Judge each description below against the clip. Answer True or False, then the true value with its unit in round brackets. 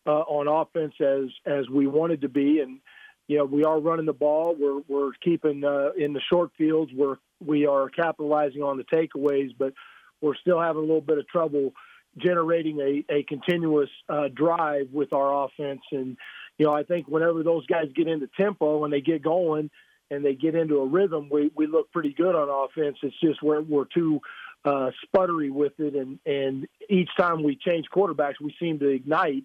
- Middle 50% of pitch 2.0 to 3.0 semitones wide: True (2.6 semitones)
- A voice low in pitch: False (150 Hz)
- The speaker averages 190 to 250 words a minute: True (200 wpm)